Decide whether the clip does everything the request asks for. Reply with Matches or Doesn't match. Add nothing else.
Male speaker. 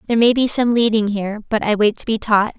Doesn't match